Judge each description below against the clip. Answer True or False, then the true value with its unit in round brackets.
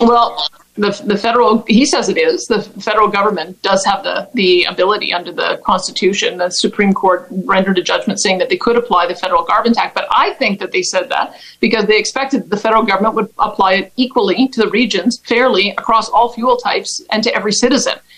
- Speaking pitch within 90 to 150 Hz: False (215 Hz)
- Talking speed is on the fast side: True (210 wpm)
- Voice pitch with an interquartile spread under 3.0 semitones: False (3.7 semitones)